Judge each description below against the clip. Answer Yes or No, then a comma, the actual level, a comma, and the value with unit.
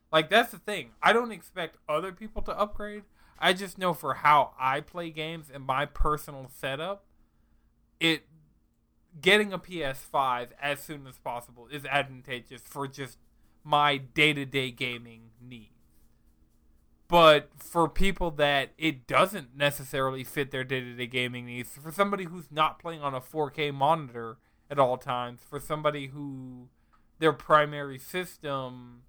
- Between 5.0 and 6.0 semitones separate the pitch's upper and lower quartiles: No, average, 4.0 semitones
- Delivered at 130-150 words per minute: Yes, average, 140 wpm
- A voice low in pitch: No, medium, 145 Hz